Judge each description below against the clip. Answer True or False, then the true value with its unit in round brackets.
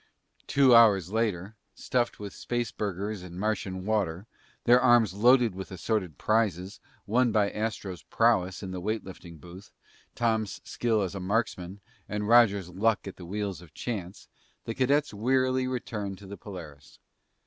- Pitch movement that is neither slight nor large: True (3.7 semitones)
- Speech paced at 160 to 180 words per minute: False (150 wpm)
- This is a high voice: False (105 Hz)